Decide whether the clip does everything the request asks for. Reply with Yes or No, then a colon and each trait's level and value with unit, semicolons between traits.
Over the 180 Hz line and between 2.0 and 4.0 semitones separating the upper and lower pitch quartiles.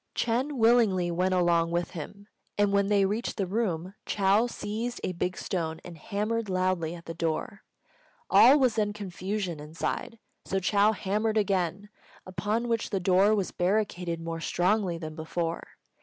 Yes: high, 190 Hz; average, 3.6 semitones